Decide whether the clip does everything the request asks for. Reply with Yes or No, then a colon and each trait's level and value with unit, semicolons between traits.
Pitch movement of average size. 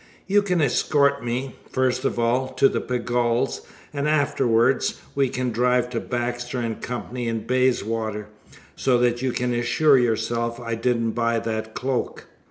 No: narrow, 1.9 semitones